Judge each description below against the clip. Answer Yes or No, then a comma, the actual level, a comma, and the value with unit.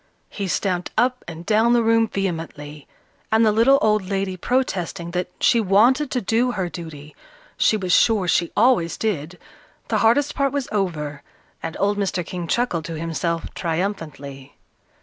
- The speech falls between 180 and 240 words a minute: No, average, 160 wpm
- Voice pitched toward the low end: No, high, 195 Hz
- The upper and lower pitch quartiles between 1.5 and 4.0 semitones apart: No, average, 5.1 semitones